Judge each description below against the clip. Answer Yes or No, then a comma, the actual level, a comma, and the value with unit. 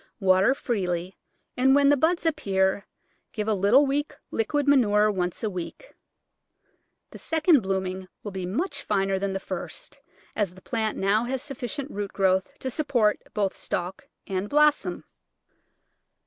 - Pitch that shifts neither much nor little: No, wide, 6.4 semitones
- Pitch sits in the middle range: No, high, 210 Hz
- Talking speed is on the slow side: No, average, 150 wpm